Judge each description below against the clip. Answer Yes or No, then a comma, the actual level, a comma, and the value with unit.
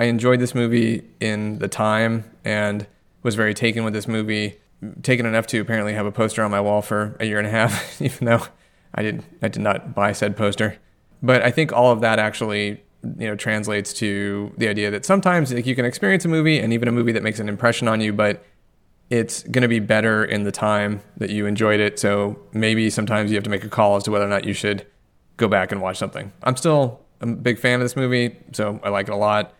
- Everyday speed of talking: No, fast, 240 wpm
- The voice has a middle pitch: No, low, 110 Hz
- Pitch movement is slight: Yes, narrow, 2.3 semitones